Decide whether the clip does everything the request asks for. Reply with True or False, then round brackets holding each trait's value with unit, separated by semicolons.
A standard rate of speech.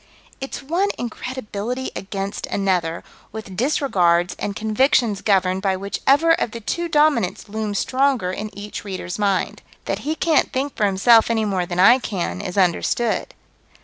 True (150 wpm)